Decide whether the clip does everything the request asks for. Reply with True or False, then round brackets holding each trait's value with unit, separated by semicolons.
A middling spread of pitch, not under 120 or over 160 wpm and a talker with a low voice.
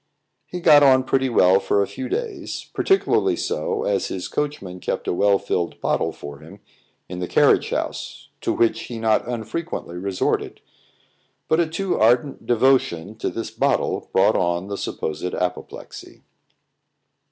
False (8.5 semitones; 150 wpm; 115 Hz)